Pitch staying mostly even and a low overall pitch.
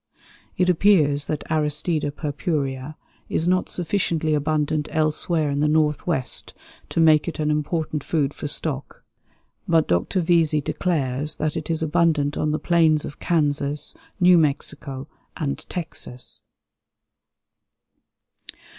No: narrow, 2.2 semitones; medium, 155 Hz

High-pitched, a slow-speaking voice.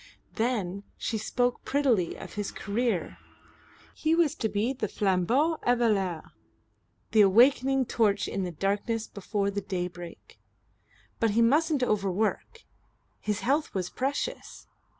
Yes: high, 220 Hz; slow, 125 wpm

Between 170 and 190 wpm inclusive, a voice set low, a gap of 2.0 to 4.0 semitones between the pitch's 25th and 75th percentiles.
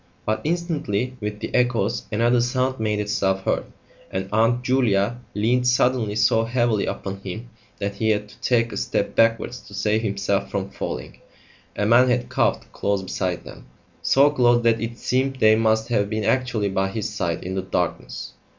Yes: average, 180 wpm; low, 110 Hz; average, 3.3 semitones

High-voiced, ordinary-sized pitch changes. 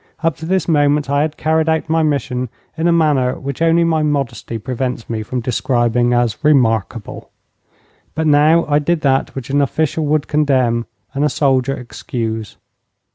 No: medium, 140 Hz; average, 3.9 semitones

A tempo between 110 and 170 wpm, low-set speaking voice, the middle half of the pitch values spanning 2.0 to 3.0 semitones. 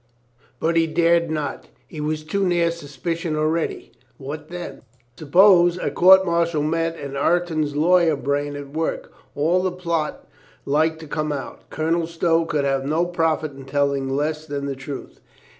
No: average, 165 wpm; medium, 160 Hz; average, 2.7 semitones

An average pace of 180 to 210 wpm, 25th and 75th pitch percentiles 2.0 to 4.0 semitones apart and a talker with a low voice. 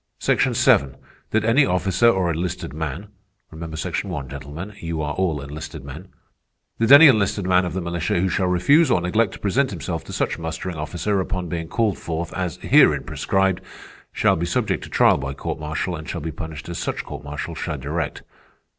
Yes: average, 190 wpm; average, 3.3 semitones; very low, 85 Hz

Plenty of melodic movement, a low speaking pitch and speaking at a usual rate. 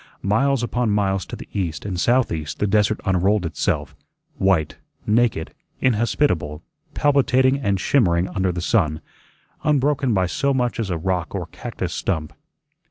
Yes: wide, 5.9 semitones; low, 100 Hz; average, 145 wpm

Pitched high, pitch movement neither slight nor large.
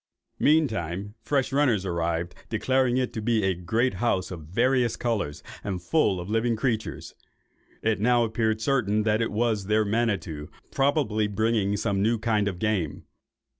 No: low, 110 Hz; average, 3.7 semitones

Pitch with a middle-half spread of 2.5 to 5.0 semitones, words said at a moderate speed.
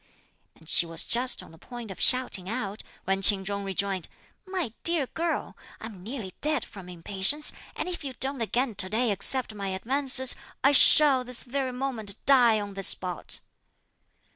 No: wide, 5.4 semitones; average, 170 wpm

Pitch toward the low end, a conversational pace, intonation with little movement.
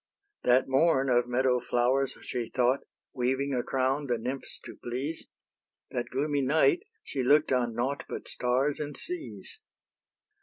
Yes: low, 130 Hz; average, 145 wpm; narrow, 2.3 semitones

